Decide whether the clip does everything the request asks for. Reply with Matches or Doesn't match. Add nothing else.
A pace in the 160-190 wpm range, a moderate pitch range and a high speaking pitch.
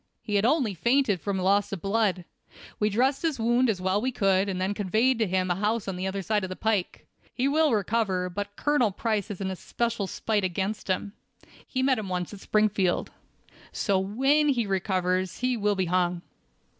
Doesn't match